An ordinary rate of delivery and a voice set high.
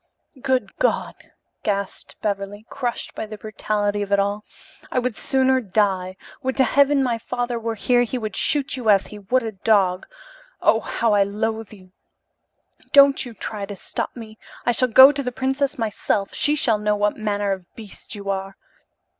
Yes: average, 180 wpm; high, 220 Hz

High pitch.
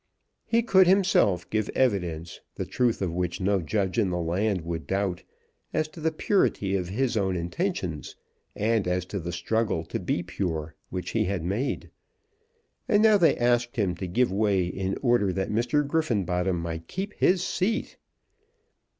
No: low, 100 Hz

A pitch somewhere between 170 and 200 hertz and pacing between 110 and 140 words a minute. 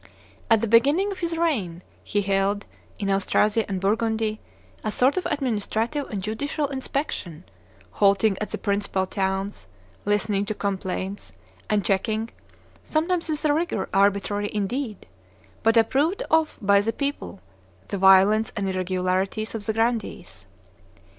No: high, 215 Hz; slow, 135 wpm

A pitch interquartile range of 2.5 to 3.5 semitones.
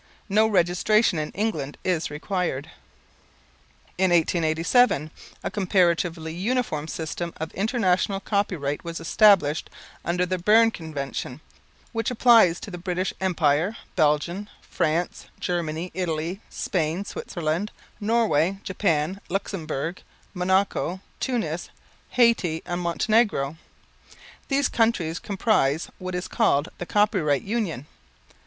No: average, 4.4 semitones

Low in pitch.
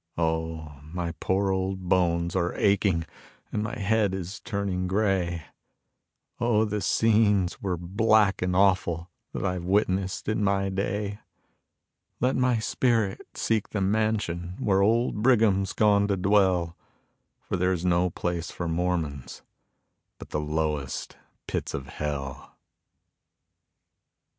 Yes: very low, 95 Hz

